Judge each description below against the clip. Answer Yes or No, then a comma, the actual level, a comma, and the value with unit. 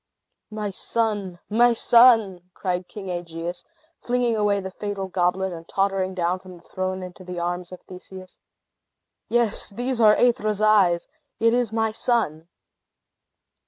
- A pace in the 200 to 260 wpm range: No, average, 150 wpm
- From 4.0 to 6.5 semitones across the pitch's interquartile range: No, average, 3.5 semitones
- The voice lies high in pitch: Yes, high, 195 Hz